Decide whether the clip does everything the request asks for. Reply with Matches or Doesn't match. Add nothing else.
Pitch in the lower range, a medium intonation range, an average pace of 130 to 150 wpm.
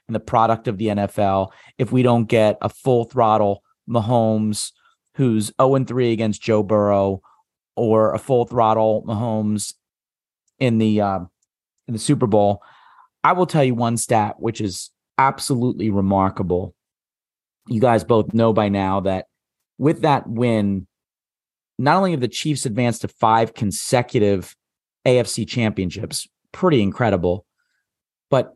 Matches